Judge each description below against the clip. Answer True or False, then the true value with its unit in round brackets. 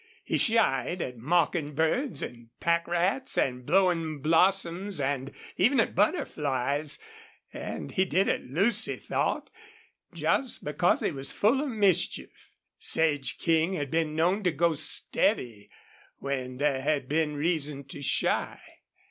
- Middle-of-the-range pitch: True (160 Hz)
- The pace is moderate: False (130 wpm)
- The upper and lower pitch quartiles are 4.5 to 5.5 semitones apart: True (4.8 semitones)